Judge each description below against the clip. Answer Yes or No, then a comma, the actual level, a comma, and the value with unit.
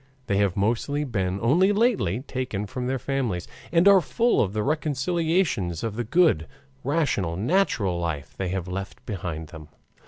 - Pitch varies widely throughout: Yes, wide, 8.6 semitones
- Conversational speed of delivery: Yes, average, 160 wpm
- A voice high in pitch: No, low, 115 Hz